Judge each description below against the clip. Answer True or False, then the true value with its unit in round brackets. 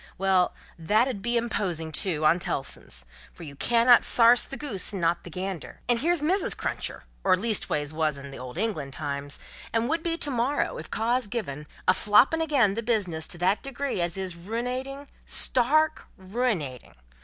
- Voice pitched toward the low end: False (205 Hz)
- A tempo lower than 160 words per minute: False (180 wpm)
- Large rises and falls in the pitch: True (7.0 semitones)